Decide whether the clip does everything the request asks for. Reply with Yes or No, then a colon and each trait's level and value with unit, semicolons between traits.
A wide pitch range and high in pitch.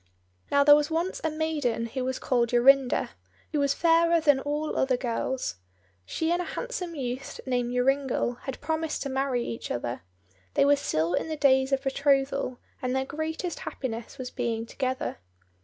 No: average, 3.3 semitones; very high, 270 Hz